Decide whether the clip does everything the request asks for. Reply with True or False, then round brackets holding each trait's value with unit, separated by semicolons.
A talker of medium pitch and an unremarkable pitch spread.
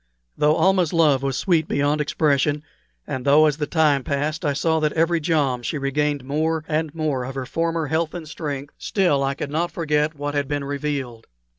False (150 Hz; 2.2 semitones)